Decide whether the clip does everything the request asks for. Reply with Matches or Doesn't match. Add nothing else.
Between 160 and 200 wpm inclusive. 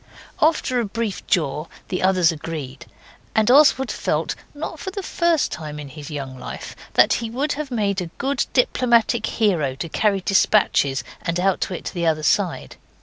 Matches